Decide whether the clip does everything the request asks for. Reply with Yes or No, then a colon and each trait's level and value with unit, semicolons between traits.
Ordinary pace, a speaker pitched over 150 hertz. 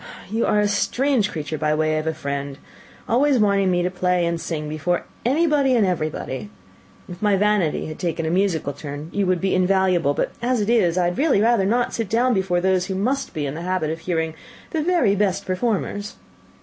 No: fast, 215 wpm; medium, 185 Hz